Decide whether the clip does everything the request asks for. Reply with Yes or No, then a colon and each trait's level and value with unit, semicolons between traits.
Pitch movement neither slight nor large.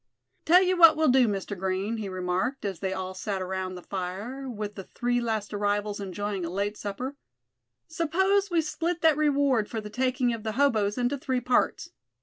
No: wide, 5.8 semitones